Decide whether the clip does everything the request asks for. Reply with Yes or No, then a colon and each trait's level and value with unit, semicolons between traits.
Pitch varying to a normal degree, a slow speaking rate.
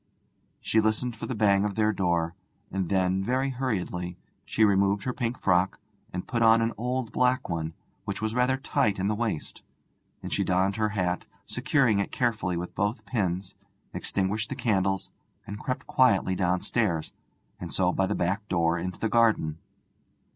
No: average, 3.9 semitones; average, 170 wpm